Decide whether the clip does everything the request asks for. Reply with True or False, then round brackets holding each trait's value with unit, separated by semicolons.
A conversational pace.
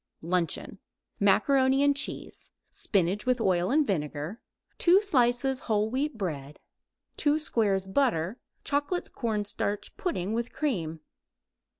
False (115 wpm)